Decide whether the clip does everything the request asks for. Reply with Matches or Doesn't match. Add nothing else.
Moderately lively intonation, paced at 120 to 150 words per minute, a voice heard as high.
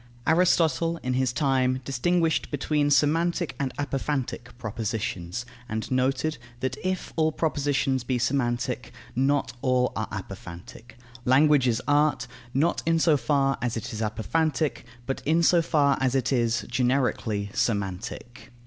Doesn't match